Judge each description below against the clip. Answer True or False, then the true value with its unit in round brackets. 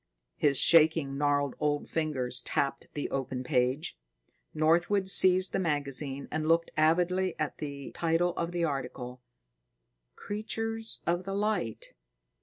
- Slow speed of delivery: True (125 wpm)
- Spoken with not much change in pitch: False (4.2 semitones)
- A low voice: False (155 Hz)